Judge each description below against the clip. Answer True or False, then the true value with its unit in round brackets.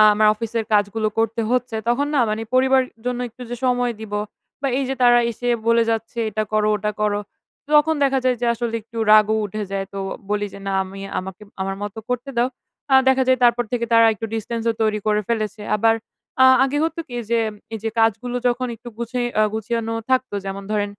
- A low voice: False (230 Hz)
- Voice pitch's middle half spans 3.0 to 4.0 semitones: False (2.6 semitones)